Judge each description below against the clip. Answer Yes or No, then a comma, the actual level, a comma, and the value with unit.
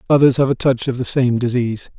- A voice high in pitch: No, low, 125 Hz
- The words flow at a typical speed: No, fast, 240 wpm